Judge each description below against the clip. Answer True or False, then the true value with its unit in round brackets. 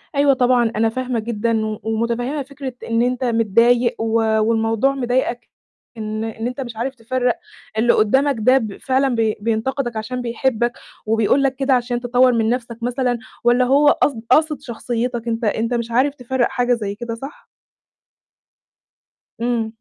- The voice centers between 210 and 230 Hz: False (240 Hz)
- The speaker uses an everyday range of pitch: False (2.3 semitones)